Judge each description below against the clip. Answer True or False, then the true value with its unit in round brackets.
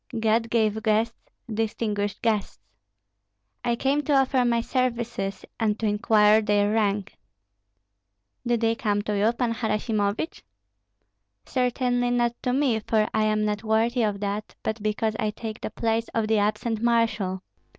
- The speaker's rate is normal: True (150 wpm)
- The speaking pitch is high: True (220 Hz)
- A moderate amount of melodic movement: False (2.0 semitones)